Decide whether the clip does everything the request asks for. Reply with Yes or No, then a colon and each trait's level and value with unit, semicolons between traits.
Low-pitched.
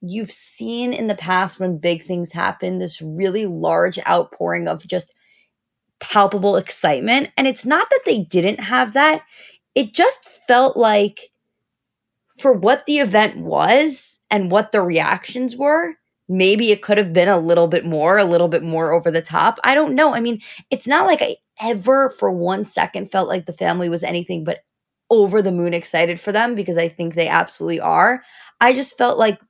No: high, 205 Hz